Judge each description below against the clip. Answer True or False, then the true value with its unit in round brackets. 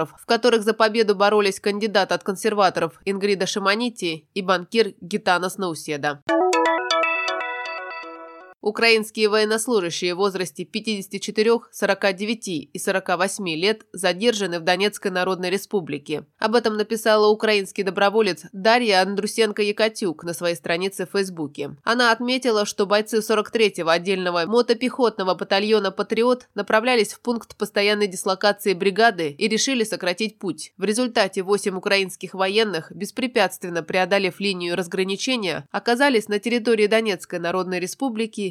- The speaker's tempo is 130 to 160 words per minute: False (115 wpm)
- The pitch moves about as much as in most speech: True (3.2 semitones)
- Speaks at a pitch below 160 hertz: False (200 Hz)